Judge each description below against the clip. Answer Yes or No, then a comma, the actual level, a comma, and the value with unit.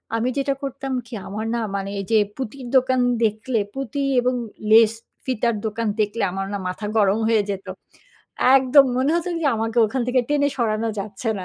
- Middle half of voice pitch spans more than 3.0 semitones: Yes, average, 3.5 semitones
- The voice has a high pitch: Yes, high, 230 Hz